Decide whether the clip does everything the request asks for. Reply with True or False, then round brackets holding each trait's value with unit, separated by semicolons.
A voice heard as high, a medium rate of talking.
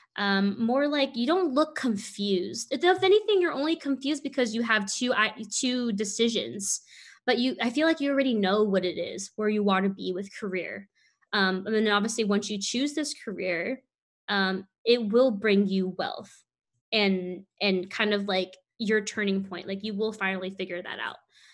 True (215 Hz; 190 wpm)